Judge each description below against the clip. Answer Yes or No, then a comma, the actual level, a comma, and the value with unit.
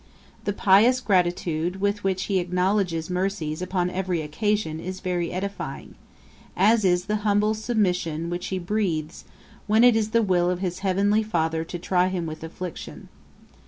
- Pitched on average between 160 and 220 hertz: Yes, medium, 185 Hz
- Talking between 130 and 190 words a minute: Yes, average, 160 wpm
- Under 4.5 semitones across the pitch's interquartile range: Yes, average, 2.9 semitones